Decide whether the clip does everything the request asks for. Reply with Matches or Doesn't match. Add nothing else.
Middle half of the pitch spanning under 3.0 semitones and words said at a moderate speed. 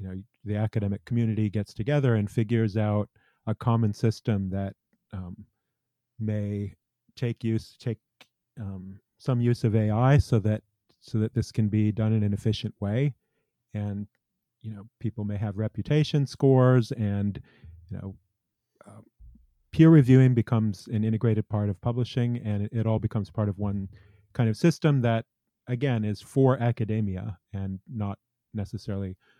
Matches